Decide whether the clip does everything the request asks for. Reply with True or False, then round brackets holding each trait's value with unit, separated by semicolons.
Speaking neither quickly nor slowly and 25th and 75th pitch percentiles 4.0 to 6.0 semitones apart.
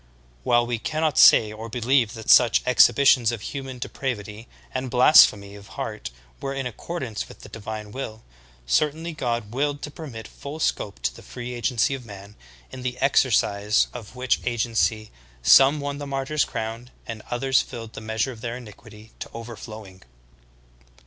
False (165 wpm; 3.6 semitones)